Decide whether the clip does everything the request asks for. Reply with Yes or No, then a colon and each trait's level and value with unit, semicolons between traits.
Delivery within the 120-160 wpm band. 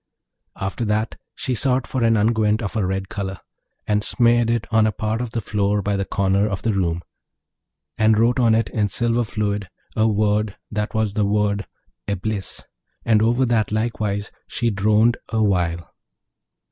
No: average, 170 wpm